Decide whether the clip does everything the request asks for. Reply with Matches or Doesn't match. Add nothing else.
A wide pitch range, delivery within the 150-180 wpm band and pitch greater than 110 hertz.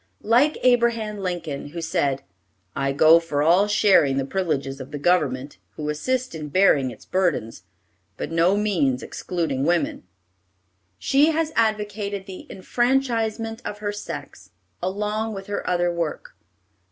Doesn't match